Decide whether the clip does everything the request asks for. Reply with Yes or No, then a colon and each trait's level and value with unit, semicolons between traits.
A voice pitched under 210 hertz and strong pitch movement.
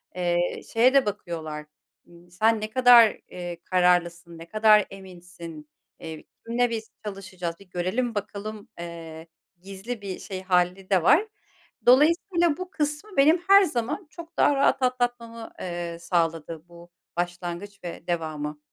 Yes: high, 190 Hz; wide, 5.8 semitones